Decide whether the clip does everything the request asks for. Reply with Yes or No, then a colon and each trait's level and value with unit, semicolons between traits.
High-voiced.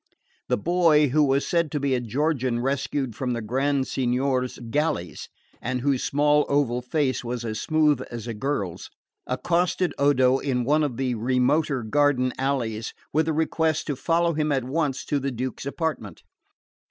No: low, 135 Hz